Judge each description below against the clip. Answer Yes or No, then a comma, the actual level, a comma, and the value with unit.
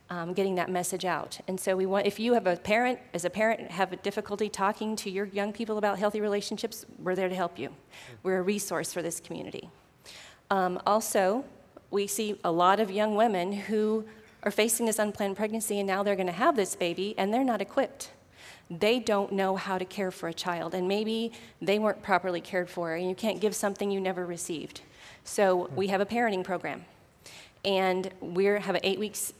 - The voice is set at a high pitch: Yes, high, 195 Hz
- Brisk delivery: Yes, fast, 210 wpm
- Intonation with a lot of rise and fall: No, narrow, 2.6 semitones